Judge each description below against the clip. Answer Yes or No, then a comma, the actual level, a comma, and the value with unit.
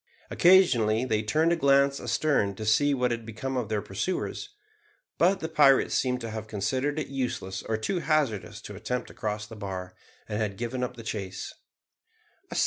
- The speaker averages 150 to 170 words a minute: No, average, 180 wpm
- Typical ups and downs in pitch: Yes, average, 4.6 semitones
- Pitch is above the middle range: No, low, 120 Hz